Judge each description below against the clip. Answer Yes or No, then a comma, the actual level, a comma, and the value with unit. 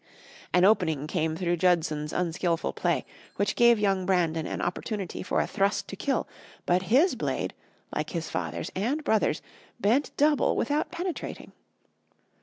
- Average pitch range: No, wide, 5.8 semitones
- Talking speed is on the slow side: No, average, 145 wpm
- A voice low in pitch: No, medium, 185 Hz